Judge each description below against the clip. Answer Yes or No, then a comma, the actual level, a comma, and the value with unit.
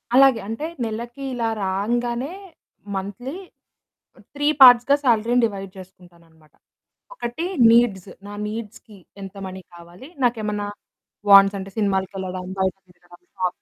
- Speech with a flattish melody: No, average, 4.2 semitones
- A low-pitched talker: No, high, 205 Hz